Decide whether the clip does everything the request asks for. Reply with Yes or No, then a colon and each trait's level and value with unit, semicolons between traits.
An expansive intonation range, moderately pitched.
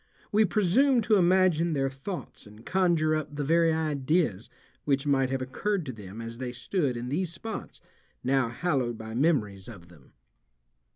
Yes: wide, 6.3 semitones; medium, 145 Hz